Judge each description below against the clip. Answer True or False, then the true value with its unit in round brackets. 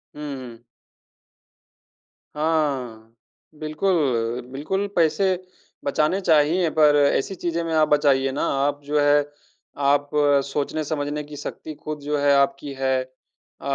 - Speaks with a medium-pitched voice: True (145 Hz)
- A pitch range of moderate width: False (2.1 semitones)